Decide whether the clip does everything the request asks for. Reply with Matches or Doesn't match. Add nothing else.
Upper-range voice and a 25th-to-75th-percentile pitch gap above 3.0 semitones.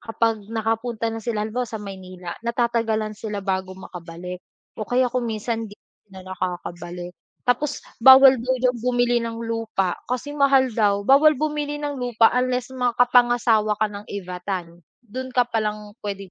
Matches